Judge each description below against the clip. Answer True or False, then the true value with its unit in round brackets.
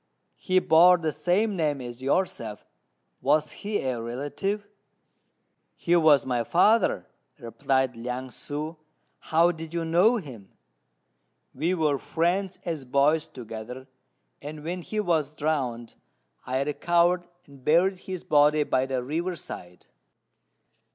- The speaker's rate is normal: False (125 wpm)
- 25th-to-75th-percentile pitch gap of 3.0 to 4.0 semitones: False (5.0 semitones)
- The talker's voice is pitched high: False (155 Hz)